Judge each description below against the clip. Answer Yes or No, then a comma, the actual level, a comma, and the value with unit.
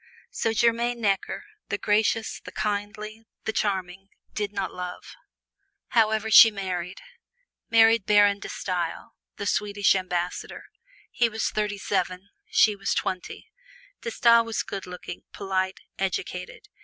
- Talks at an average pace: No, slow, 130 wpm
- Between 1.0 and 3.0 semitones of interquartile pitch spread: Yes, average, 2.7 semitones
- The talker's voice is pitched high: Yes, high, 205 Hz